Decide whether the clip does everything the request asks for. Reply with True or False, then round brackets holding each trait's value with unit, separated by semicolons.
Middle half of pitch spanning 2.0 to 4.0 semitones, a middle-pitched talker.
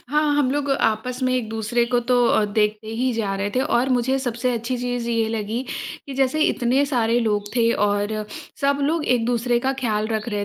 False (2.9 semitones; 240 Hz)